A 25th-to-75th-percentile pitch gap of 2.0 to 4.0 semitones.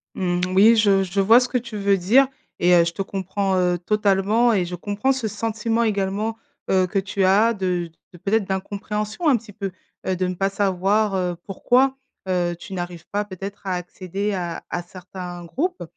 Yes: average, 2.8 semitones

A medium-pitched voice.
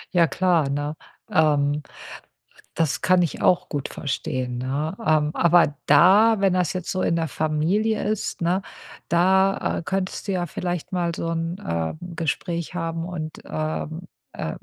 Yes: medium, 165 Hz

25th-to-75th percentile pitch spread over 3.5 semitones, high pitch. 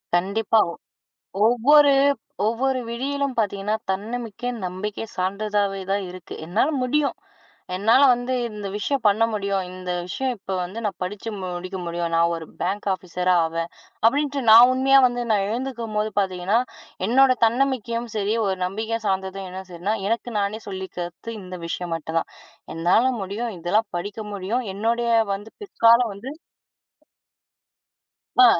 Yes: average, 4.0 semitones; high, 210 Hz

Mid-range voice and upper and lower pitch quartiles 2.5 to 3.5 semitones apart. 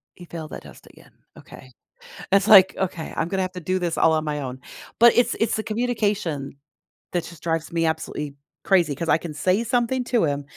No: medium, 175 Hz; average, 4.8 semitones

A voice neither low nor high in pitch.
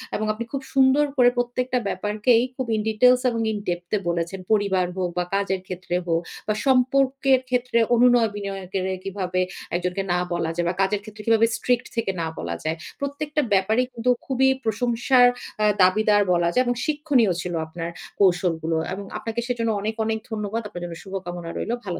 No: high, 215 Hz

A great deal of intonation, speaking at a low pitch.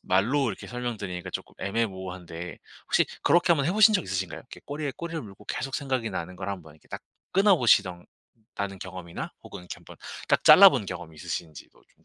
Yes: wide, 7.2 semitones; low, 100 Hz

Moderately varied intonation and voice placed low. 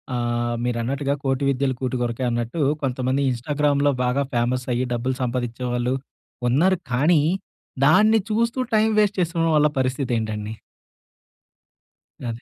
Yes: average, 3.6 semitones; low, 130 Hz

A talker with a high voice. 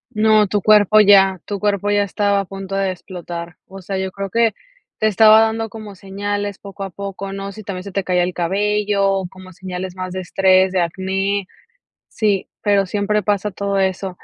Yes: high, 195 Hz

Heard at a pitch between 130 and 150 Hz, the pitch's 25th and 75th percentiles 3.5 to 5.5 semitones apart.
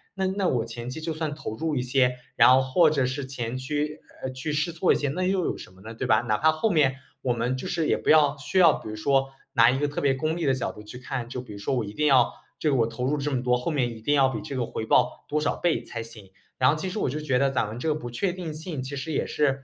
Yes: low, 135 Hz; average, 3.9 semitones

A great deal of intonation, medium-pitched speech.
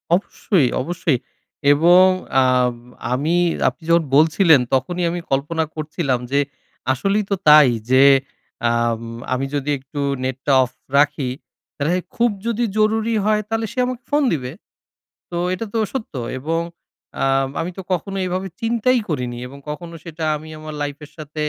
Yes: wide, 5.8 semitones; medium, 160 Hz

